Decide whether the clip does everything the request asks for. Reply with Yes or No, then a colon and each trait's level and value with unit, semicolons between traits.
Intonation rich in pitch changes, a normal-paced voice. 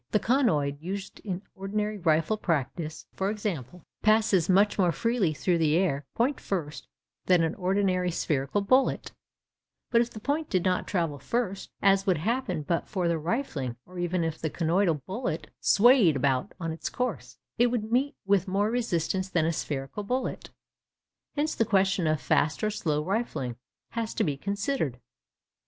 No: average, 5.0 semitones; average, 165 wpm